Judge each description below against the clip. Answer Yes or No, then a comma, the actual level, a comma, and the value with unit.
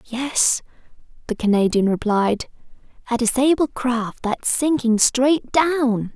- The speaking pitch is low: No, high, 245 Hz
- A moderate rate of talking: No, slow, 105 wpm